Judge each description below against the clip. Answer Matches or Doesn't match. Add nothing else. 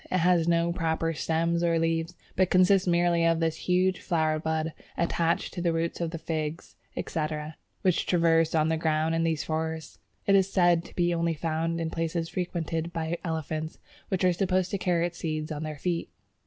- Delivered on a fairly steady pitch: Matches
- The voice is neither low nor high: Matches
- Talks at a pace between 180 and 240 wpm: Matches